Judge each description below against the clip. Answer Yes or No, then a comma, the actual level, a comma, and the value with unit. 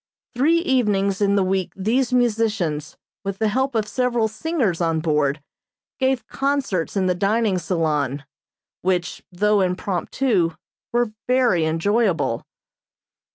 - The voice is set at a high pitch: Yes, high, 200 Hz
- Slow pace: Yes, slow, 120 wpm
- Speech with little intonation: No, wide, 5.6 semitones